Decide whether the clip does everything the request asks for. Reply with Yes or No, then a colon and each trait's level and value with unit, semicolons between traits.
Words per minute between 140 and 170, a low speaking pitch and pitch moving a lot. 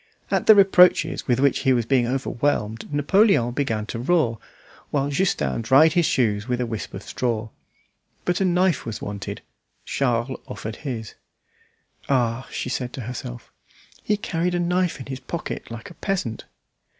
Yes: average, 160 wpm; low, 130 Hz; wide, 6.6 semitones